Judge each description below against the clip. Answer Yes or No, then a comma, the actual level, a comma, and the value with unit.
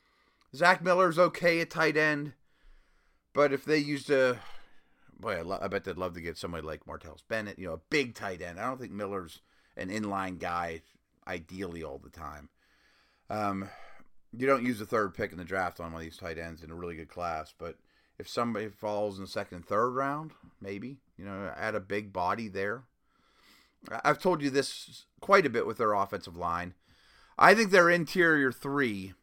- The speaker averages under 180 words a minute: No, average, 195 wpm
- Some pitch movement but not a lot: No, wide, 8.1 semitones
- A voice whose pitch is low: Yes, low, 105 Hz